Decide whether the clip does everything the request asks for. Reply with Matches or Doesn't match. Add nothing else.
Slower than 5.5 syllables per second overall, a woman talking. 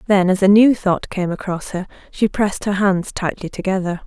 Matches